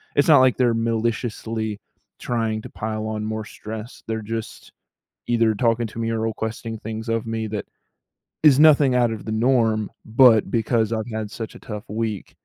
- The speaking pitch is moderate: No, low, 115 Hz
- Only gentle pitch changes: Yes, narrow, 1.2 semitones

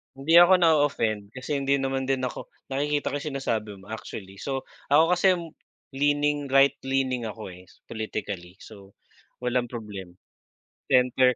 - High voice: No, low, 130 Hz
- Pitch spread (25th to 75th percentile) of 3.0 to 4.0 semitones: No, average, 4.7 semitones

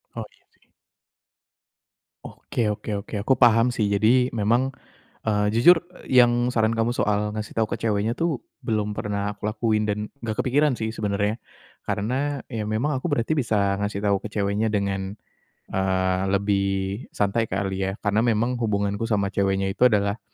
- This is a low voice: Yes, low, 105 Hz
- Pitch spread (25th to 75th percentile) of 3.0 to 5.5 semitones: No, narrow, 2.6 semitones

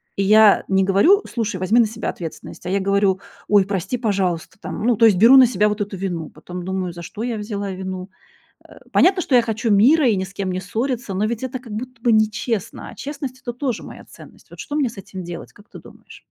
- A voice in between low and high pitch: No, high, 210 Hz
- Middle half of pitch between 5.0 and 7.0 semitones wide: No, average, 4.0 semitones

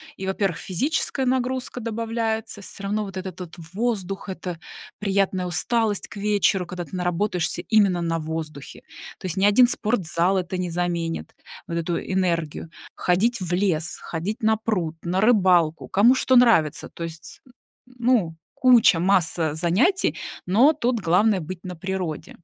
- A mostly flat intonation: No, average, 4.3 semitones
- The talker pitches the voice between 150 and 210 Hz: Yes, high, 190 Hz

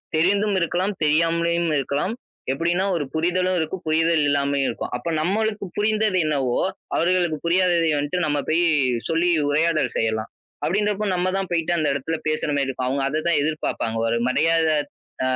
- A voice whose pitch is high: No, medium, 165 Hz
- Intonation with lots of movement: No, average, 3.8 semitones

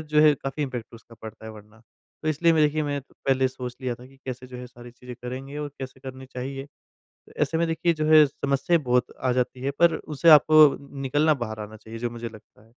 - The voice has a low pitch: Yes, low, 130 Hz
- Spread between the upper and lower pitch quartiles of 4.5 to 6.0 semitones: No, average, 3.6 semitones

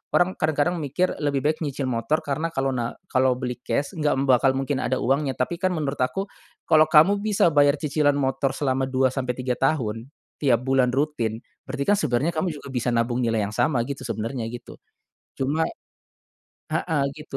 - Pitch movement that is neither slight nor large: Yes, average, 3.0 semitones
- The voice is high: No, medium, 140 Hz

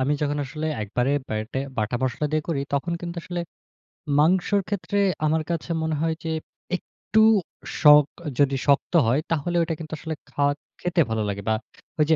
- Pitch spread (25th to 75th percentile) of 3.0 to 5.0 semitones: Yes, average, 3.5 semitones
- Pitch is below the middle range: No, medium, 150 Hz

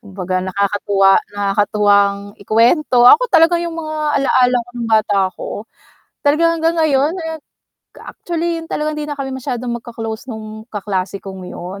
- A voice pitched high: Yes, high, 235 Hz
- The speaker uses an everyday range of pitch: No, wide, 6.9 semitones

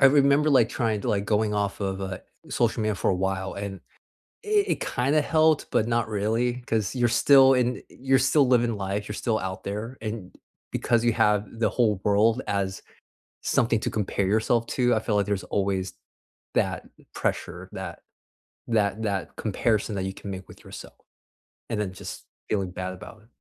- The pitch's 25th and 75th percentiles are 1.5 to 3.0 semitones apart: No, average, 3.4 semitones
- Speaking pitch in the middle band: No, low, 110 Hz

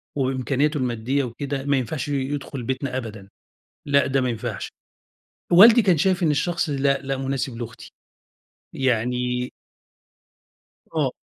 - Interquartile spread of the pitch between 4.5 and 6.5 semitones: No, narrow, 2.4 semitones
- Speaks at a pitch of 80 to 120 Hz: No, low, 135 Hz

